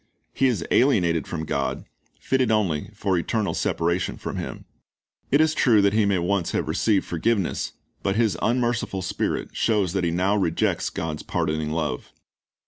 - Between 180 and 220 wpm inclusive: No, average, 165 wpm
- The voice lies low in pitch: Yes, very low, 95 Hz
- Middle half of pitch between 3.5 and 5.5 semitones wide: Yes, average, 5.0 semitones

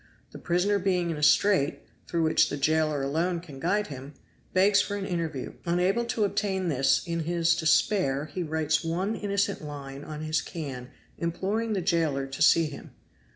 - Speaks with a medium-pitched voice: Yes, medium, 165 Hz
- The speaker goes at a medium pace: Yes, average, 175 wpm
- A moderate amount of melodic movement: Yes, average, 4.3 semitones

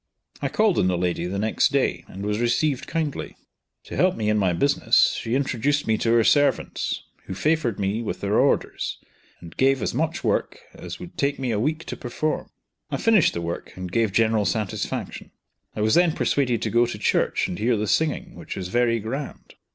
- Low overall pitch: Yes, low, 115 Hz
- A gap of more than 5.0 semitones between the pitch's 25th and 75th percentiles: Yes, wide, 5.6 semitones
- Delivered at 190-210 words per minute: Yes, fast, 205 wpm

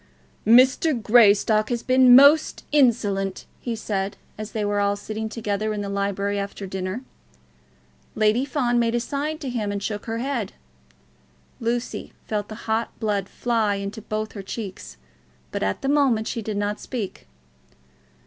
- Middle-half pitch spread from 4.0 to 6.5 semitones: No, average, 3.1 semitones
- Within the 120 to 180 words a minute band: Yes, average, 160 wpm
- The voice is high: Yes, high, 215 Hz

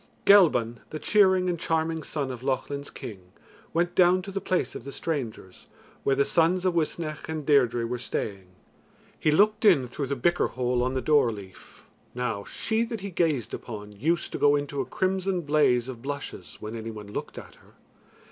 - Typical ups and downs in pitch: No, wide, 6.2 semitones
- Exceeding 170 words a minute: Yes, average, 190 wpm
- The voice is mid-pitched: Yes, medium, 145 Hz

